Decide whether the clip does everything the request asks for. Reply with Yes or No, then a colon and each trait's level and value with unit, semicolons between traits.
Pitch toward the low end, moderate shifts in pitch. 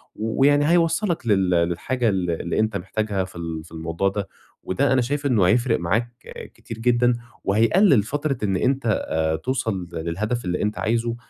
No: low, 110 Hz; wide, 5.9 semitones